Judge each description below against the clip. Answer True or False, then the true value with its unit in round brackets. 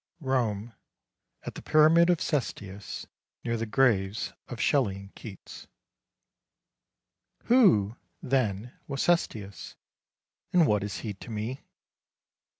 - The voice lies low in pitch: True (115 Hz)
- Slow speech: True (110 wpm)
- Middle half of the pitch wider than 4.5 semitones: True (5.2 semitones)